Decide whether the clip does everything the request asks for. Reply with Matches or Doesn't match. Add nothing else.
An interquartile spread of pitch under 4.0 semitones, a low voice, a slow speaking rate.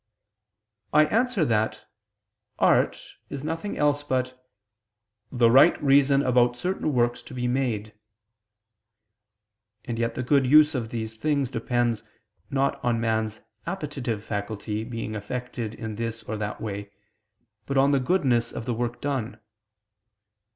Matches